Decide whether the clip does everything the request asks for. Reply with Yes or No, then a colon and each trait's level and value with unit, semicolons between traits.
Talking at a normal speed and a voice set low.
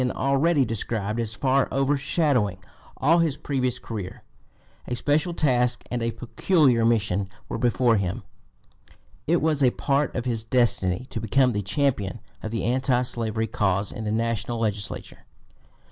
Yes: average, 150 wpm; low, 120 Hz